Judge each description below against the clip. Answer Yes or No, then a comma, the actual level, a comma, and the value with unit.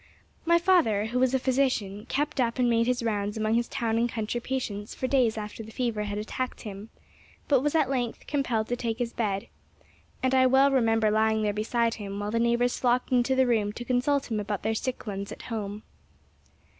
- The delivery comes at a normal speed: No, fast, 210 wpm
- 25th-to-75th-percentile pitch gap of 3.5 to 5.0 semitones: No, average, 3.1 semitones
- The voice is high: Yes, high, 235 Hz